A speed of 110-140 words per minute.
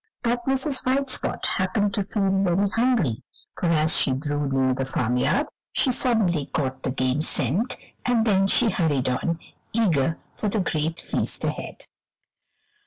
No: average, 155 wpm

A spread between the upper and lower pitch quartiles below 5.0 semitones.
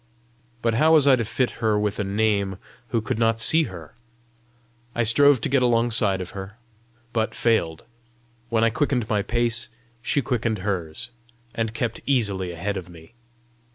Yes: average, 3.3 semitones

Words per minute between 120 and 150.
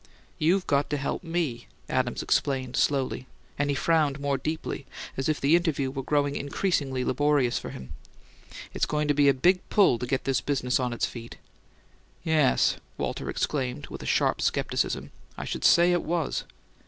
No: average, 175 wpm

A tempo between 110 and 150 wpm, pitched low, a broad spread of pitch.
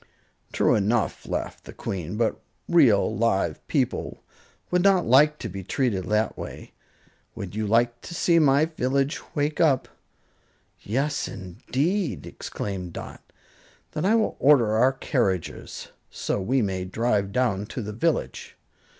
Yes: average, 140 wpm; low, 120 Hz; wide, 6.6 semitones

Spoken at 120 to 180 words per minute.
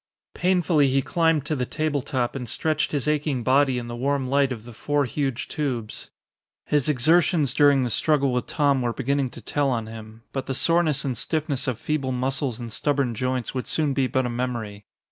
No: average, 200 wpm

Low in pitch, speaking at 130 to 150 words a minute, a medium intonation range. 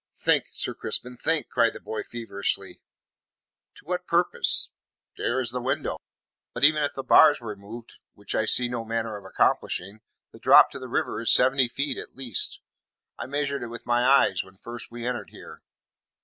No: low, 120 Hz; average, 185 wpm; average, 3.2 semitones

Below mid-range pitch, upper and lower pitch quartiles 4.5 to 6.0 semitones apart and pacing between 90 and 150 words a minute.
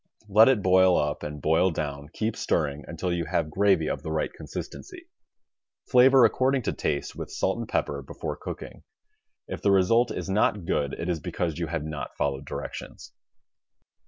No: very low, 85 Hz; average, 5.1 semitones; average, 175 wpm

